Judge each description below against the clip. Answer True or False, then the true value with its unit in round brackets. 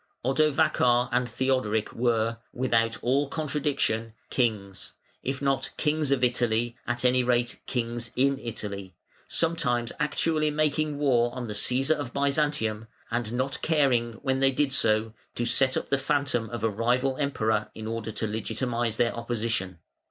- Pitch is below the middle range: True (125 Hz)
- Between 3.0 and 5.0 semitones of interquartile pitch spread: True (3.4 semitones)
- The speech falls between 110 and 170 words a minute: True (150 wpm)